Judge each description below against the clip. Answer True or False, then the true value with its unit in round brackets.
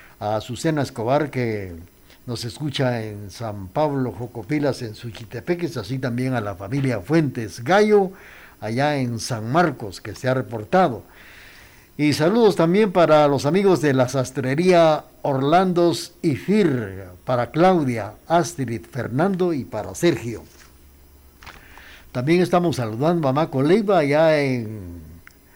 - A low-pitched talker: True (130 Hz)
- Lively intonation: True (6.9 semitones)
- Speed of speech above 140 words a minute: False (125 wpm)